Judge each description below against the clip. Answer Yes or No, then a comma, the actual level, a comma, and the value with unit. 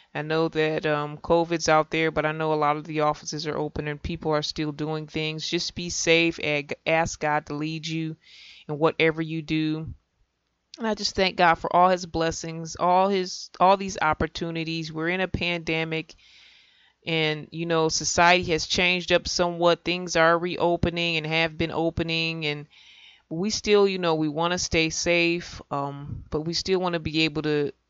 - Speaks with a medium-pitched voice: Yes, medium, 160 Hz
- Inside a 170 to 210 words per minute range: Yes, average, 190 wpm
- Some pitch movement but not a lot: No, narrow, 1.8 semitones